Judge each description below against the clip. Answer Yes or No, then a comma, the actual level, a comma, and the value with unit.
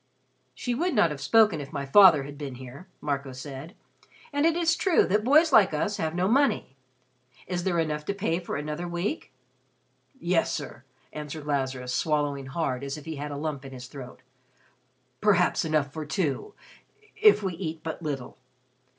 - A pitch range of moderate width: No, wide, 5.7 semitones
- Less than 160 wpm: No, average, 175 wpm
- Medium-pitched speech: Yes, medium, 155 Hz